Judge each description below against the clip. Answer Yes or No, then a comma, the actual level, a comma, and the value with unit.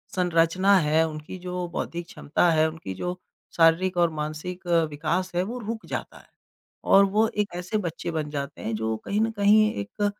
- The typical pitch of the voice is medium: Yes, medium, 175 Hz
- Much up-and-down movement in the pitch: No, average, 3.8 semitones